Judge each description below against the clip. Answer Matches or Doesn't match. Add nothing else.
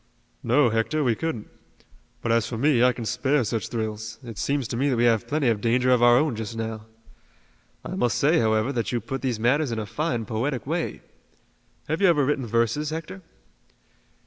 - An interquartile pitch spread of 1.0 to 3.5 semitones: Doesn't match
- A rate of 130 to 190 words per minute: Doesn't match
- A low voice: Matches